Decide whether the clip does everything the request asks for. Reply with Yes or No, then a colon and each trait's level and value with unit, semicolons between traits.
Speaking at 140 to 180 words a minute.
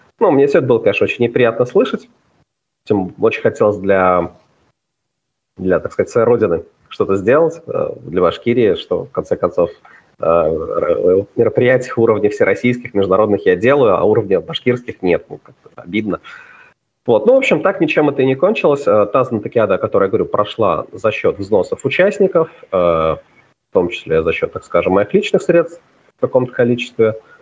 Yes: fast, 160 wpm